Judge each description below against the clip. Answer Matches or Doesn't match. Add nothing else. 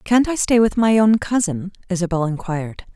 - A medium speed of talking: Matches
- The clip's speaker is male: Doesn't match